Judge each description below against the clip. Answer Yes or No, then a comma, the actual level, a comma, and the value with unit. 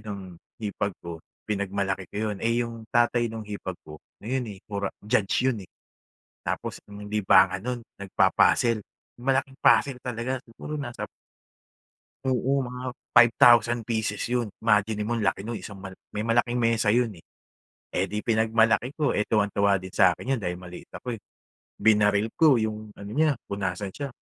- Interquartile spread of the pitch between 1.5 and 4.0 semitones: Yes, average, 3.2 semitones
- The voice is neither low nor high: No, low, 110 Hz